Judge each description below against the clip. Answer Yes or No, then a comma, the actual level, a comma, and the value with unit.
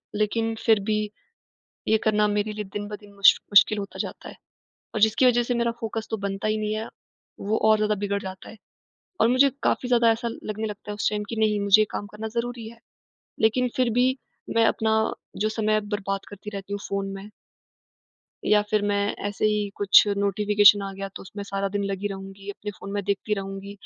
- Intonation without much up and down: Yes, narrow, 1.6 semitones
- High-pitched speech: Yes, high, 210 Hz